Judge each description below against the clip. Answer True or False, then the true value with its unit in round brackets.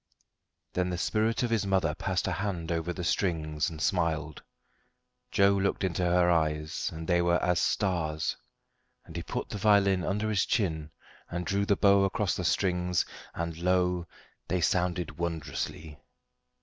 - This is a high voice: False (90 Hz)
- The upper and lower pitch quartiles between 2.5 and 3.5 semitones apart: True (3.0 semitones)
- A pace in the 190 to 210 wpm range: False (165 wpm)